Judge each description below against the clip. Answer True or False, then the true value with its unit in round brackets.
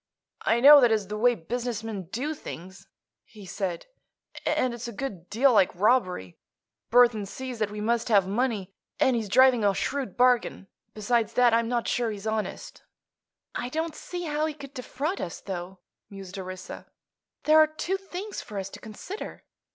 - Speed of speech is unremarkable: True (175 wpm)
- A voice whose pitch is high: True (230 Hz)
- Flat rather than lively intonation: False (4.7 semitones)